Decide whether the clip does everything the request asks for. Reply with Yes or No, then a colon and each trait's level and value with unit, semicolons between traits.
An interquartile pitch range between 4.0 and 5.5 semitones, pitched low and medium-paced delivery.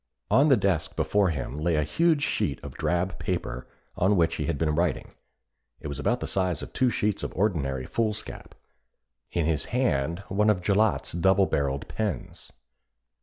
Yes: average, 5.2 semitones; very low, 90 Hz; average, 170 wpm